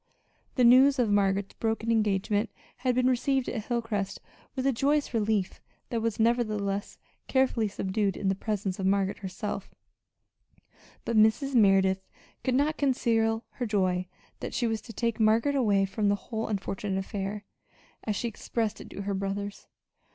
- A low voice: No, high, 215 Hz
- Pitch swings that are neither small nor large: Yes, average, 3.2 semitones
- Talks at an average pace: Yes, average, 160 wpm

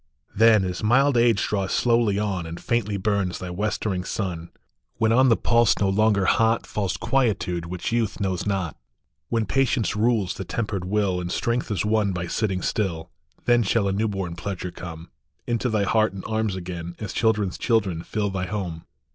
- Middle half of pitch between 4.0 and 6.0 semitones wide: No, average, 3.5 semitones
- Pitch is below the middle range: Yes, low, 100 Hz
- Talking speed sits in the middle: Yes, average, 190 wpm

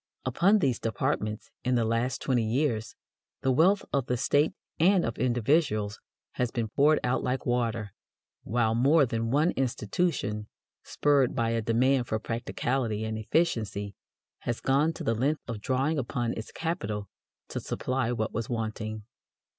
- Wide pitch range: No, average, 3.7 semitones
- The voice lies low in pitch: Yes, low, 120 Hz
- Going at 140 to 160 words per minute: Yes, average, 155 wpm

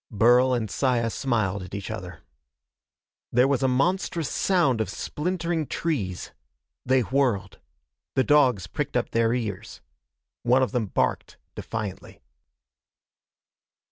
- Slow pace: Yes, slow, 120 wpm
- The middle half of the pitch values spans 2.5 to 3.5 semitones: No, average, 4.2 semitones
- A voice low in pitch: Yes, low, 125 Hz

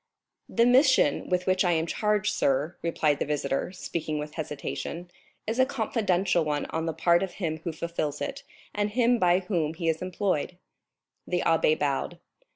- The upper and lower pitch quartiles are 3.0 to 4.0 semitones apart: No, average, 4.5 semitones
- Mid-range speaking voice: Yes, medium, 175 Hz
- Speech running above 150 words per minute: Yes, average, 170 wpm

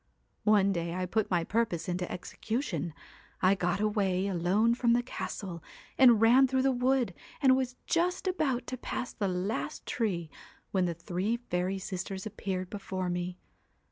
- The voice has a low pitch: No, high, 200 Hz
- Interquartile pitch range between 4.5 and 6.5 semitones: Yes, average, 5.0 semitones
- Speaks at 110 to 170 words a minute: Yes, average, 165 wpm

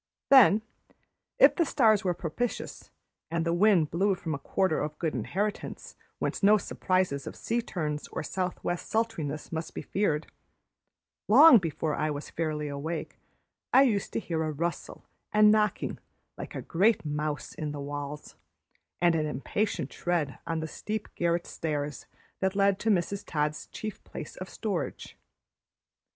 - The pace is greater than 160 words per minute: No, average, 155 wpm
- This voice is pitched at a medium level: Yes, medium, 170 Hz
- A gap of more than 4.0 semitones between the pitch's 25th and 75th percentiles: Yes, average, 5.2 semitones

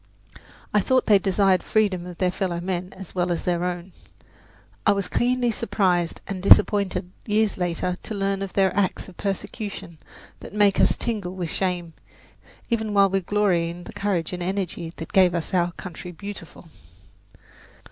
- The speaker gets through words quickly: No, average, 170 wpm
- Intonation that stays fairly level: Yes, narrow, 2.3 semitones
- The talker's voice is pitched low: No, high, 190 Hz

